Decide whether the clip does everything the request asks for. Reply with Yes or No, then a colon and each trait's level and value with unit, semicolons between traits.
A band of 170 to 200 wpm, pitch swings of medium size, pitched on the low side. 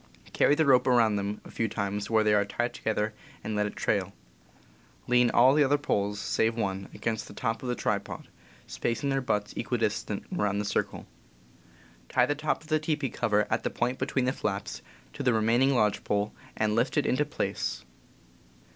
Yes: average, 190 wpm; average, 4.0 semitones; low, 115 Hz